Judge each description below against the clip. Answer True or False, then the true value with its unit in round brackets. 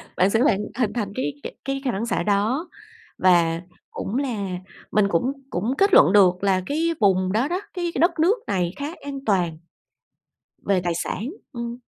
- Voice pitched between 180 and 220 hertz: True (210 Hz)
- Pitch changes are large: True (6.5 semitones)